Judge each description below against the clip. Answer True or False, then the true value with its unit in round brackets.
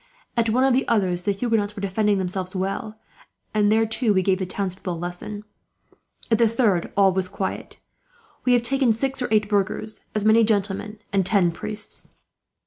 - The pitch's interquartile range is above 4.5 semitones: False (2.8 semitones)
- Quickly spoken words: False (185 wpm)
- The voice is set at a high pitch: True (210 Hz)